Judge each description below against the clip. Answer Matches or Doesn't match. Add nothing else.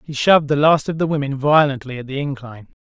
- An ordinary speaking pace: Doesn't match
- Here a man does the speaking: Matches